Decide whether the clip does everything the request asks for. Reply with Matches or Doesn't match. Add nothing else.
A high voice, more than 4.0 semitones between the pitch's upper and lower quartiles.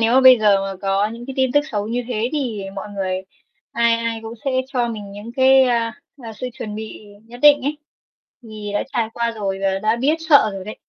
Doesn't match